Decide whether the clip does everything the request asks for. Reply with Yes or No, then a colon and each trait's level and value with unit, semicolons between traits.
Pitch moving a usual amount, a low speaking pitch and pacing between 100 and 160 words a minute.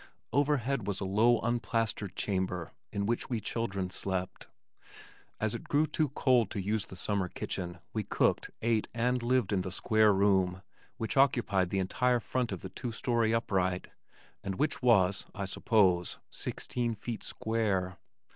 Yes: average, 4.0 semitones; low, 110 Hz; average, 155 wpm